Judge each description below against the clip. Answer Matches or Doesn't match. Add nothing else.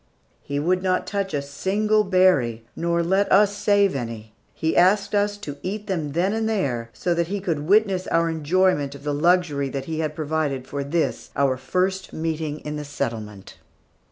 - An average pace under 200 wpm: Matches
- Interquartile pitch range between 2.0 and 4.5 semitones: Doesn't match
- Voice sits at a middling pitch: Matches